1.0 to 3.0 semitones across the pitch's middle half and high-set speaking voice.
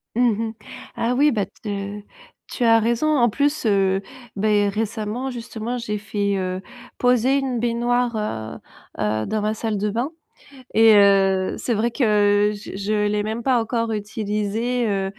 Yes: average, 2.7 semitones; high, 220 Hz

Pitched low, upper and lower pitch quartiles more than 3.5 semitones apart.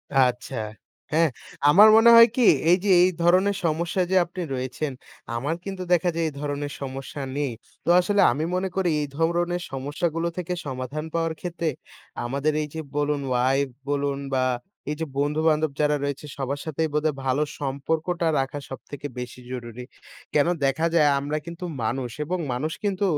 No: medium, 150 Hz; average, 3.9 semitones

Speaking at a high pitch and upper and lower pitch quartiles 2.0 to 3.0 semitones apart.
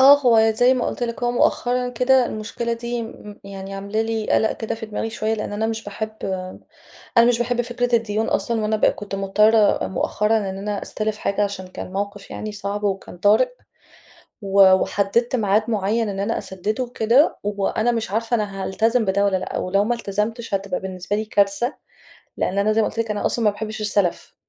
Yes: high, 215 Hz; narrow, 2.5 semitones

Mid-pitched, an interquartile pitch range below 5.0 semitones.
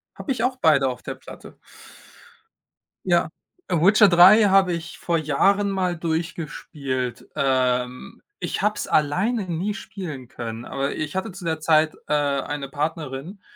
No: medium, 160 Hz; wide, 5.5 semitones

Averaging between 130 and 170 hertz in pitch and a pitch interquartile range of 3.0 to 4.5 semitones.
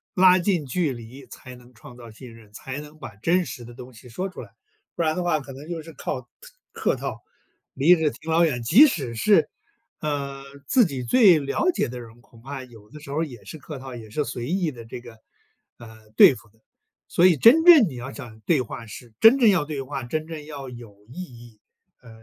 No: low, 135 Hz; wide, 5.5 semitones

